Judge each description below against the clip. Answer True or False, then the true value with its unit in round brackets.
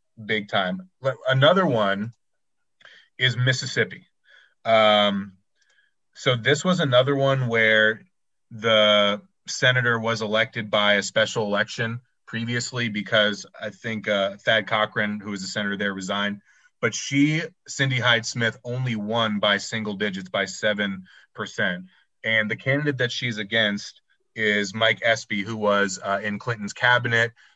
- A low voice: True (110 Hz)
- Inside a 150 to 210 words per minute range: False (135 wpm)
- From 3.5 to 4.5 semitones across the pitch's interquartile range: False (2.9 semitones)